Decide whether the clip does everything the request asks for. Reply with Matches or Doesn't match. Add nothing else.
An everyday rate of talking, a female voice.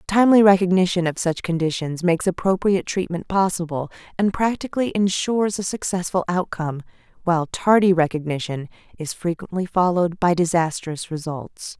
Doesn't match